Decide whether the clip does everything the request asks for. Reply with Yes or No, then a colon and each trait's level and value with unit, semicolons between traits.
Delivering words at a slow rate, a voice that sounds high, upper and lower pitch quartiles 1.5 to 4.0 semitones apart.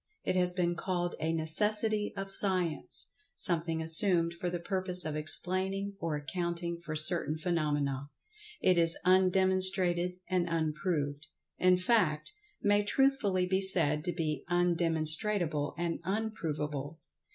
No: slow, 120 wpm; medium, 175 Hz; average, 2.9 semitones